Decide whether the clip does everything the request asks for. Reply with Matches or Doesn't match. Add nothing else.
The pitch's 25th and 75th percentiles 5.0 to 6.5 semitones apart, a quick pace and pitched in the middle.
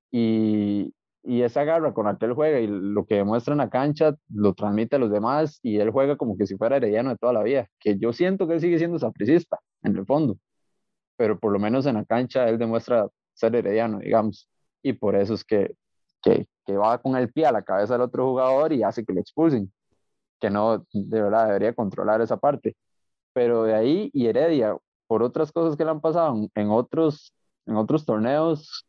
Doesn't match